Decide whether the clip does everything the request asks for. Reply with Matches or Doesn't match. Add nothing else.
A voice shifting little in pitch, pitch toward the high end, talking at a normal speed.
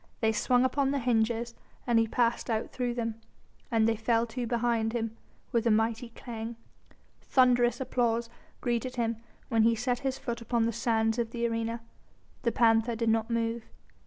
Matches